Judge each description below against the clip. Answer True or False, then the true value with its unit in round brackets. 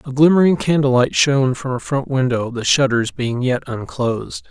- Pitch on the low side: True (130 Hz)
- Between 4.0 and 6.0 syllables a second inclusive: True (5.0 syllables/s)